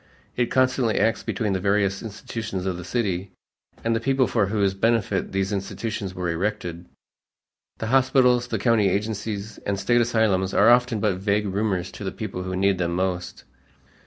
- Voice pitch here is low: Yes, low, 100 Hz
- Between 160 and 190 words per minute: Yes, average, 170 wpm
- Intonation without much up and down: No, average, 3.1 semitones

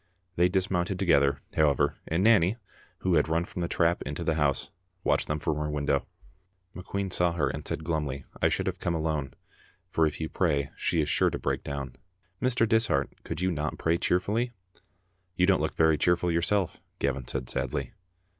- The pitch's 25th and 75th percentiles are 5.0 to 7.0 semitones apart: No, average, 3.6 semitones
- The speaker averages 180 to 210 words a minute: Yes, average, 185 wpm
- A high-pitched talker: No, very low, 80 Hz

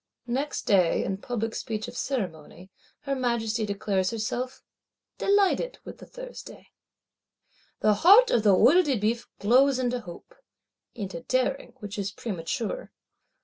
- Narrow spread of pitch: No, average, 4.5 semitones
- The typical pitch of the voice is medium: No, high, 230 Hz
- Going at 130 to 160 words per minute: Yes, slow, 135 wpm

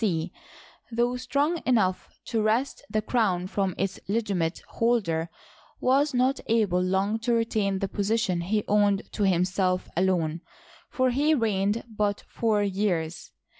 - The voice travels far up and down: No, average, 3.9 semitones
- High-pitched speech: Yes, high, 205 Hz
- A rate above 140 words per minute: No, slow, 135 wpm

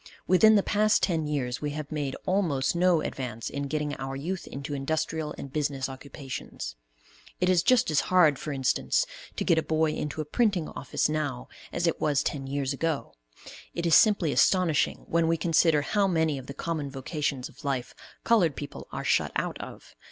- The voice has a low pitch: No, medium, 150 Hz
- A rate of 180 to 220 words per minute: Yes, average, 190 wpm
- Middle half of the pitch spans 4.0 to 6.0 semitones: No, average, 3.6 semitones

